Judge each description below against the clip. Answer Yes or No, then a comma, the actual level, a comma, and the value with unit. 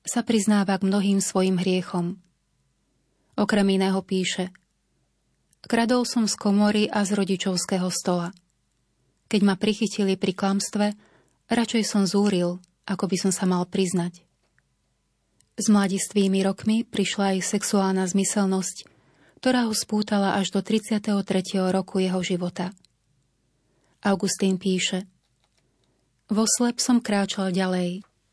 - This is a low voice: No, high, 195 Hz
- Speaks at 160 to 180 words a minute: No, average, 115 wpm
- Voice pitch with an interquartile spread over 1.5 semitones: Yes, narrow, 2.4 semitones